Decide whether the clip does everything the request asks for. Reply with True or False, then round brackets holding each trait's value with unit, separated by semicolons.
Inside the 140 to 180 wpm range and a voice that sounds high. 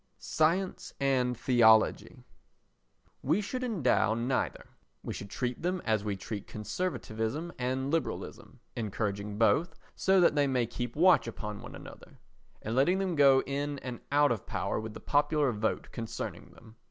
False (155 wpm; 130 Hz)